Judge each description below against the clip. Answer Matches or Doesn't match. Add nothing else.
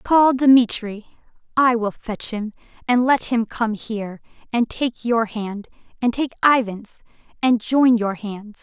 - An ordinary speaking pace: Matches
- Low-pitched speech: Doesn't match